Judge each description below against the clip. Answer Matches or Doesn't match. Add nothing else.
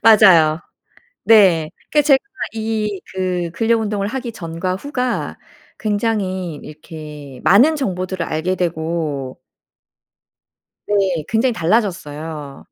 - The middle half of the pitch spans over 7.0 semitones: Doesn't match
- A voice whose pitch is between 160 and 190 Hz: Matches